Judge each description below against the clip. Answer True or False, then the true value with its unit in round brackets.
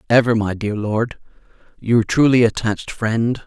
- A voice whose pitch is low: True (115 Hz)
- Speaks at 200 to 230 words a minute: False (140 wpm)